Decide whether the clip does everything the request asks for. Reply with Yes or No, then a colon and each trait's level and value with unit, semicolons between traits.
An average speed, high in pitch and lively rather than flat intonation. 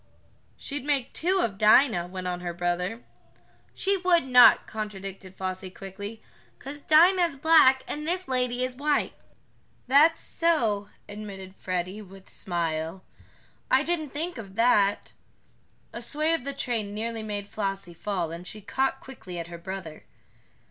Yes: average, 150 wpm; high, 215 Hz; wide, 6.7 semitones